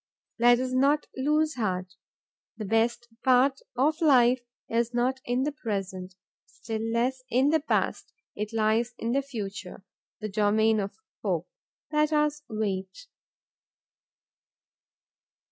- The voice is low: No, high, 240 Hz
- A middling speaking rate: No, slow, 125 wpm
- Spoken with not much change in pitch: No, average, 4.0 semitones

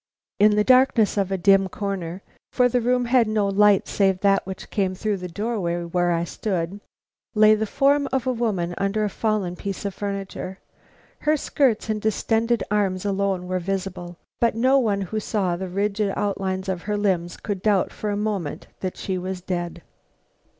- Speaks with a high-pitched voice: Yes, high, 200 Hz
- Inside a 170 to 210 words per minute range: Yes, average, 185 wpm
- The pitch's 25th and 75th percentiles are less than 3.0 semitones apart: Yes, narrow, 2.6 semitones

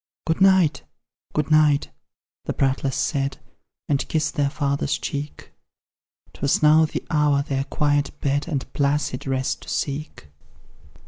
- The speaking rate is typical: No, slow, 130 wpm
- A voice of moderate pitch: Yes, medium, 145 Hz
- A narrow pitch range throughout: Yes, narrow, 1.6 semitones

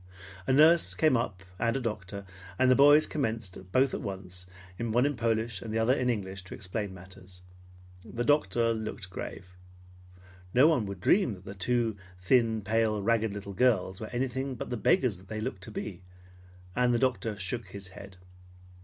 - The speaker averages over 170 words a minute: Yes, average, 180 wpm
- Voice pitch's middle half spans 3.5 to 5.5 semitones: Yes, average, 4.3 semitones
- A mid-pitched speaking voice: No, low, 110 Hz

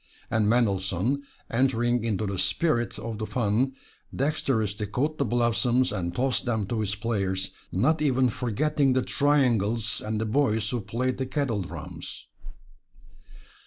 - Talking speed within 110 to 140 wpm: Yes, slow, 135 wpm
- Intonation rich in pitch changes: No, average, 3.7 semitones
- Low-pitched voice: Yes, low, 115 Hz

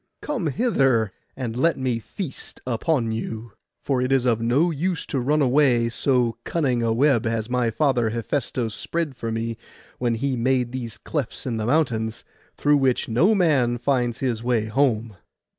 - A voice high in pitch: No, low, 125 Hz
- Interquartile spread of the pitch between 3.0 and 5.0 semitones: Yes, average, 3.5 semitones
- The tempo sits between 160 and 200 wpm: Yes, average, 170 wpm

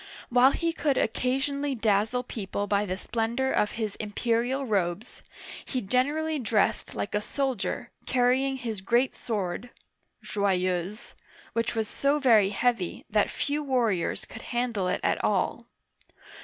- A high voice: Yes, high, 235 Hz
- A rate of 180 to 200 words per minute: No, slow, 135 wpm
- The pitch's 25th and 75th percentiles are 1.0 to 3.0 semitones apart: No, average, 4.4 semitones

